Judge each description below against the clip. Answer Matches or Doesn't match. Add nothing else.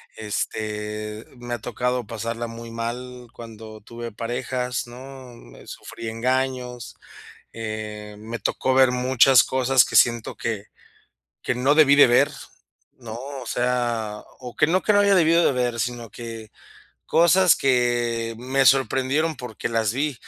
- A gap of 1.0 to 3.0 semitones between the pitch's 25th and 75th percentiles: Matches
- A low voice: Matches